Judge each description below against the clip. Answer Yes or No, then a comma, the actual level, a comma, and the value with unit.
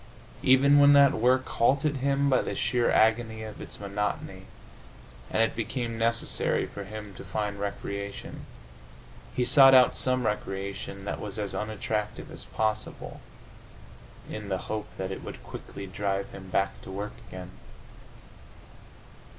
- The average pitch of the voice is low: Yes, low, 110 Hz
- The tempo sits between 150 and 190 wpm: No, average, 140 wpm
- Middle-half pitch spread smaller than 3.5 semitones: No, average, 4.0 semitones